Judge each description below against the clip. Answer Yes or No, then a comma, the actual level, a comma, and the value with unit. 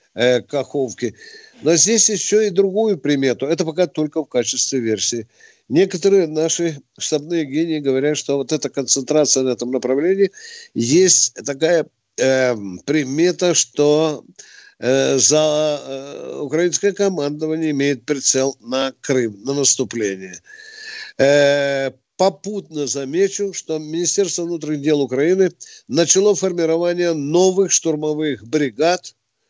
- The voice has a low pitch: No, medium, 155 Hz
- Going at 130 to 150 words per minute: No, slow, 110 wpm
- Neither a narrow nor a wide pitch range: Yes, average, 4.7 semitones